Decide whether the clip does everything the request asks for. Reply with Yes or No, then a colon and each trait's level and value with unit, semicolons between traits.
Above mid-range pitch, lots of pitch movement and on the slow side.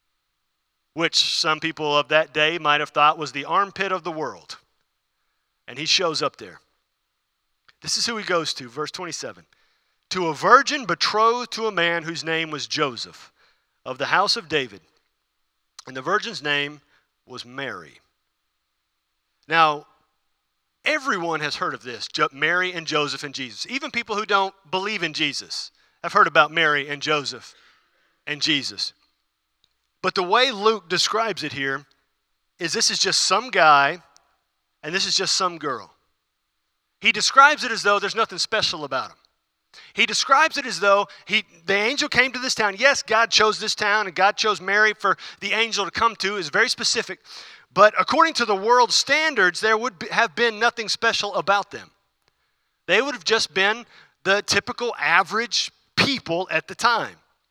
No: high, 195 Hz; wide, 6.4 semitones; average, 170 wpm